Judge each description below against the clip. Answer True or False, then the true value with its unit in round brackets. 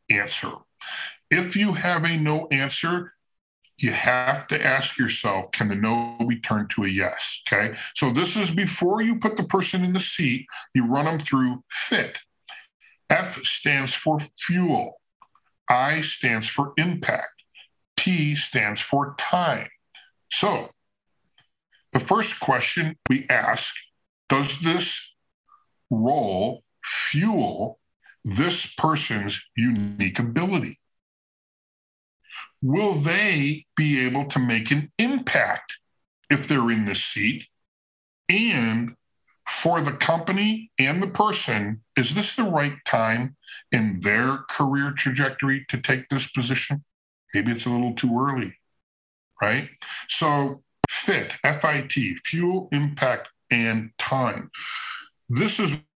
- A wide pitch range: True (5.8 semitones)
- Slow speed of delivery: True (120 wpm)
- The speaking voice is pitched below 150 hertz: True (140 Hz)